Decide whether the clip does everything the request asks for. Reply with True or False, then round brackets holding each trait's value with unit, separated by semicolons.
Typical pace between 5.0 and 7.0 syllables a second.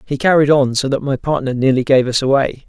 True (5.9 syllables/s)